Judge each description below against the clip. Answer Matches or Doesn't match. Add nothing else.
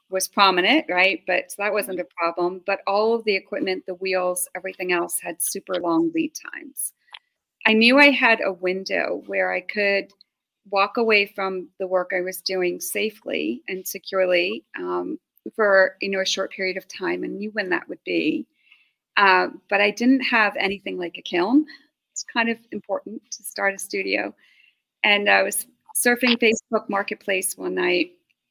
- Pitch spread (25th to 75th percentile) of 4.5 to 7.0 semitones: Matches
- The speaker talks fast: Doesn't match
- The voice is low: Doesn't match